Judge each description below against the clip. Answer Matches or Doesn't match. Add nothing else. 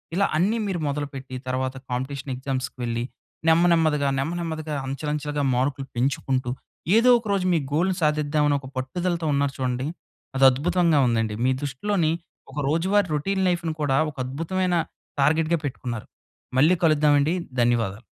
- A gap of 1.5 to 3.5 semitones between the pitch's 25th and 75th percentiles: Doesn't match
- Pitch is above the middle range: Doesn't match